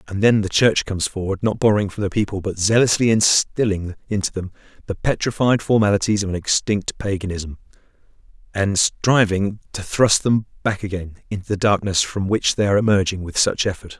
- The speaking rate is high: No, average, 175 wpm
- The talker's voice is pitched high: No, low, 100 Hz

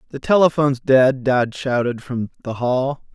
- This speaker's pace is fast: No, average, 155 wpm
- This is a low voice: Yes, low, 130 Hz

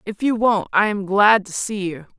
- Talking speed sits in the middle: No, fast, 245 wpm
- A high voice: Yes, high, 205 Hz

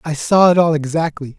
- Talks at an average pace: No, fast, 215 wpm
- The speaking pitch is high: No, medium, 155 Hz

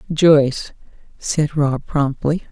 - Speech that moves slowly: Yes, slow, 95 wpm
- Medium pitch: Yes, medium, 145 Hz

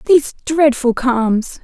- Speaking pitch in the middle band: No, very high, 265 Hz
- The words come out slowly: Yes, slow, 110 wpm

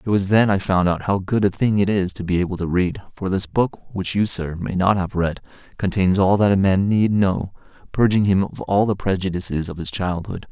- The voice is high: No, very low, 95 Hz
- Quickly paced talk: Yes, fast, 240 wpm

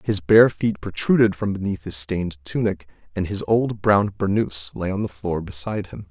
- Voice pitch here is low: Yes, very low, 95 Hz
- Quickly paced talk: No, average, 195 wpm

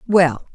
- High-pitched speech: No, medium, 175 Hz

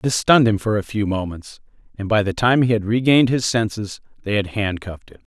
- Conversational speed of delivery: No, fast, 225 wpm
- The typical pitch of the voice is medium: No, low, 105 Hz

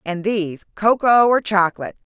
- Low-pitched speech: No, high, 205 Hz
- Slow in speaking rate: Yes, slow, 110 wpm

